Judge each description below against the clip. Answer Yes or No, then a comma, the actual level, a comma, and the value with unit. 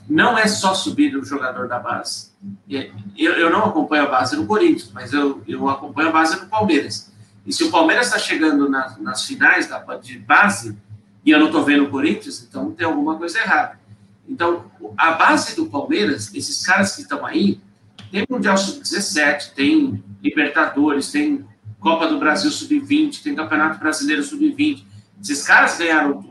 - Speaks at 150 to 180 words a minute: Yes, average, 175 wpm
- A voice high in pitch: No, medium, 155 Hz